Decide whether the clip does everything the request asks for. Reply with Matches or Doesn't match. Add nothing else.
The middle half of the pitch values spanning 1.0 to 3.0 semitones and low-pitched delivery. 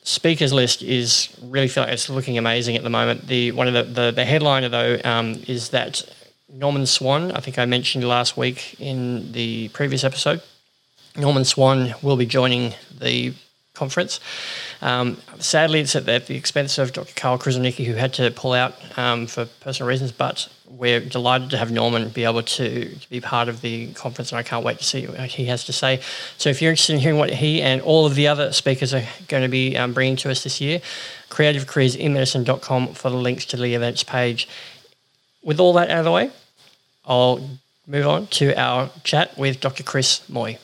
Matches